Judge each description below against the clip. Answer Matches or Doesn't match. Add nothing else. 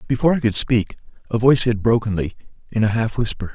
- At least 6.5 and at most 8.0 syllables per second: Matches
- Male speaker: Matches